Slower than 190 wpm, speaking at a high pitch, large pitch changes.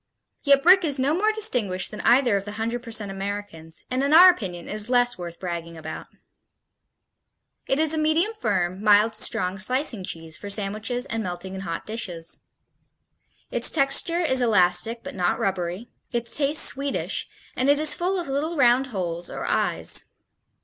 Yes: average, 170 wpm; high, 225 Hz; wide, 6.9 semitones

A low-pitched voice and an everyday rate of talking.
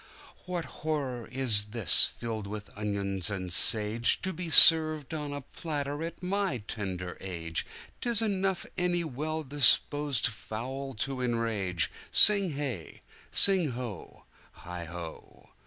No: low, 130 Hz; slow, 115 wpm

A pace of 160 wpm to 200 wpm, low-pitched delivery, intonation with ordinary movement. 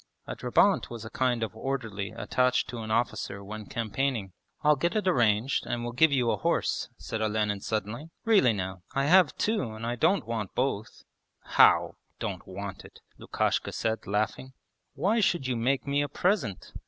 Yes: average, 180 wpm; low, 120 Hz; average, 4.4 semitones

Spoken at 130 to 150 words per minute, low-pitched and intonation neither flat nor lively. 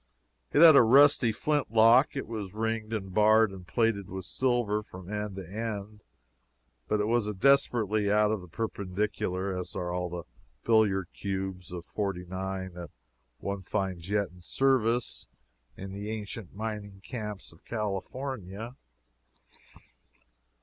Yes: average, 140 wpm; low, 105 Hz; average, 3.0 semitones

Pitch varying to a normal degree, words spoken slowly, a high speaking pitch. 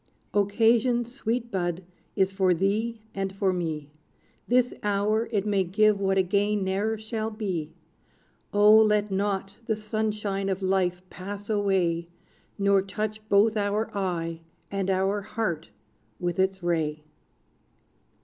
No: narrow, 2.2 semitones; slow, 130 wpm; high, 200 Hz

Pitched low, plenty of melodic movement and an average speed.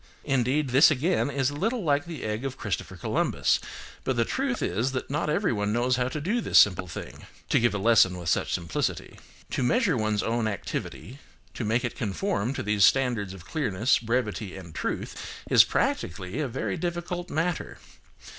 Yes: low, 125 Hz; wide, 6.1 semitones; average, 185 wpm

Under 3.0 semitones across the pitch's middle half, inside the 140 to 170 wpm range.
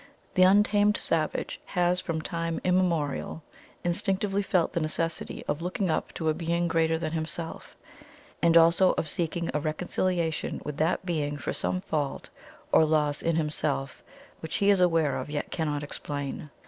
Yes: narrow, 2.6 semitones; average, 160 wpm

